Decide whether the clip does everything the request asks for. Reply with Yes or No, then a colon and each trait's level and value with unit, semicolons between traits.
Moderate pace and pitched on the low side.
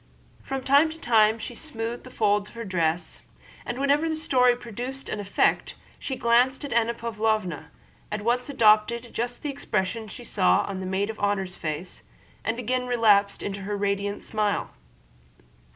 No: average, 170 wpm; high, 225 Hz